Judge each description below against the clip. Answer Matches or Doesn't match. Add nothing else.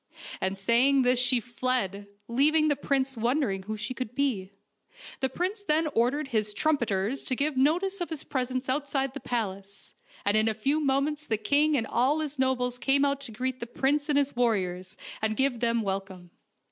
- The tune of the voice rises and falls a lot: Doesn't match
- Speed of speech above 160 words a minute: Matches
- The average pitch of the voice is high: Matches